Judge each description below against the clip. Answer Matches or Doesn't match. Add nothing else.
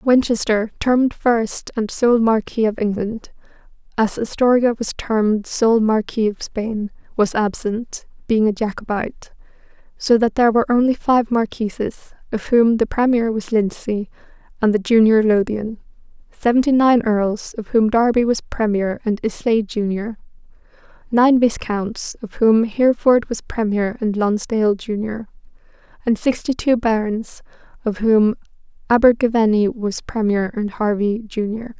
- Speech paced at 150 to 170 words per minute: Doesn't match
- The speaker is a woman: Matches